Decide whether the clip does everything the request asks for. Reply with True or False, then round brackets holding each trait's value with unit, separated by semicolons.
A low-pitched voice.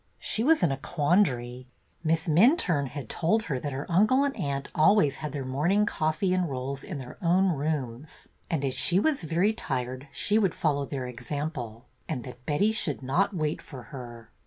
False (150 Hz)